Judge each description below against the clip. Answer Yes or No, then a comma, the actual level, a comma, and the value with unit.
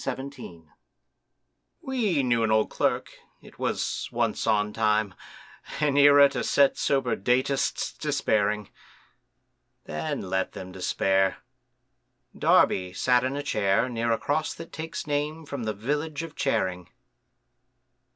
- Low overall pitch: Yes, low, 125 Hz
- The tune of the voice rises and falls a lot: Yes, wide, 5.9 semitones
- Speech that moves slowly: Yes, slow, 130 wpm